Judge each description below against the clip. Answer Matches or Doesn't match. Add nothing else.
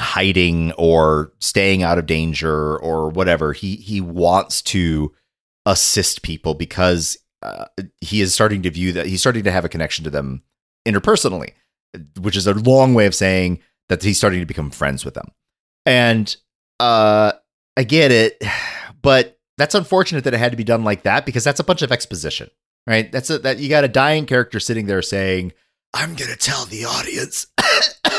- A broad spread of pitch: Matches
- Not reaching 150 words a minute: Doesn't match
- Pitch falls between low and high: Doesn't match